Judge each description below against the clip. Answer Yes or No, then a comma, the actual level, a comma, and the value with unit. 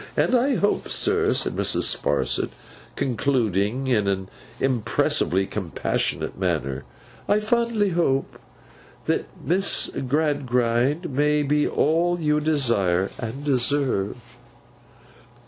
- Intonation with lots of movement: Yes, wide, 5.8 semitones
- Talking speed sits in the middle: No, slow, 100 wpm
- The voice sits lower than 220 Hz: Yes, low, 135 Hz